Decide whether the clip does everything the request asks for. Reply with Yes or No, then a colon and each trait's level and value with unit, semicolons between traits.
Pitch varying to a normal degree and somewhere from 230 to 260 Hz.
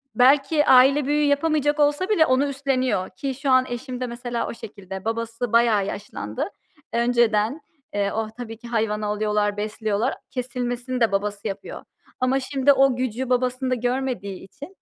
Yes: average, 3.7 semitones; high, 245 Hz